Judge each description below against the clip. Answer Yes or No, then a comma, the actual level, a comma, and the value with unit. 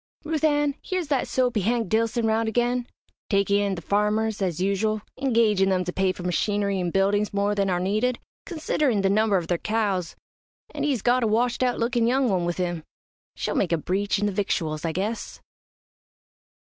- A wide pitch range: No, average, 3.9 semitones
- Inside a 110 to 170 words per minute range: No, average, 190 wpm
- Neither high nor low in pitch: No, high, 210 Hz